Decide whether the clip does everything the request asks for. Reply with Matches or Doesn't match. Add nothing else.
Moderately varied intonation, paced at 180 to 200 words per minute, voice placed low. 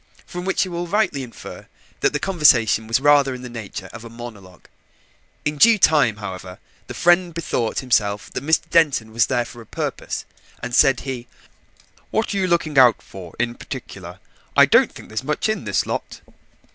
Doesn't match